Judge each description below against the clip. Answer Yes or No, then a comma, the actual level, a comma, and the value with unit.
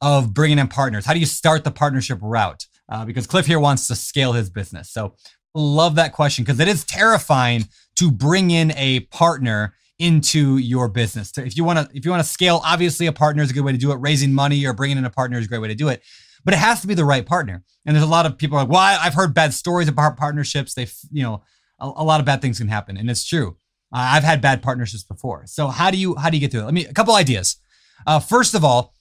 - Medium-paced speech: No, fast, 275 wpm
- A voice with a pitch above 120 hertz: Yes, medium, 140 Hz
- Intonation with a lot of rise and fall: No, average, 4.7 semitones